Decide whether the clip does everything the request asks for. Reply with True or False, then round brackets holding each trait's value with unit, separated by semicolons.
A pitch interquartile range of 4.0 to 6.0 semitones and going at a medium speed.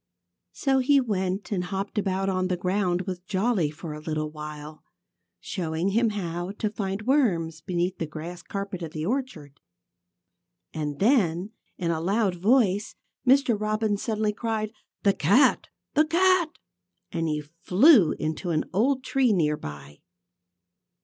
True (4.9 semitones; 145 wpm)